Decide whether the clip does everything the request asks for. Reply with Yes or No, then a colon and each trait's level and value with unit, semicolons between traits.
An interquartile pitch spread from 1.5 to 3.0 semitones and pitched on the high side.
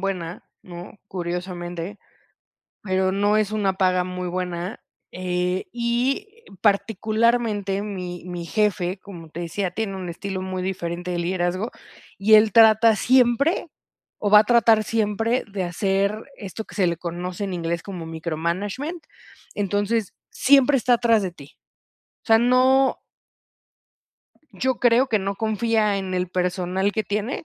No: average, 3.7 semitones; high, 195 Hz